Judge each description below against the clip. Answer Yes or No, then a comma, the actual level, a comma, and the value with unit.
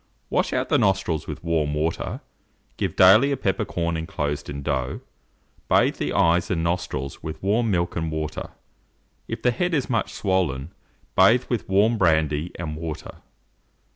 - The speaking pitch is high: No, very low, 85 Hz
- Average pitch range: Yes, average, 4.0 semitones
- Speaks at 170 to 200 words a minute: No, average, 155 wpm